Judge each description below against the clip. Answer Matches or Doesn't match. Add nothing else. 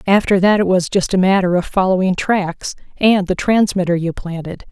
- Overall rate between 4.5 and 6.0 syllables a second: Matches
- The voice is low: Doesn't match